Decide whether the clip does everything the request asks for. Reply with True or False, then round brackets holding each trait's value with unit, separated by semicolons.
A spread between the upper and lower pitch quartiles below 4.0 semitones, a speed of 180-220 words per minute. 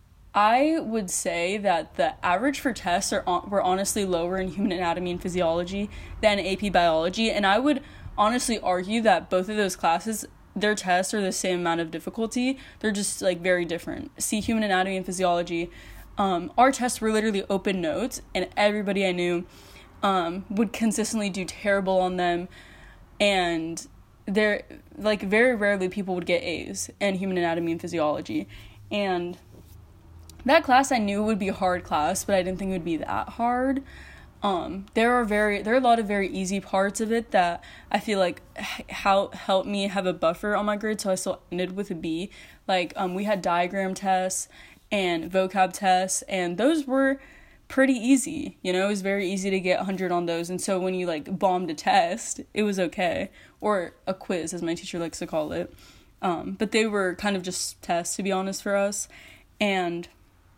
True (3.1 semitones; 190 wpm)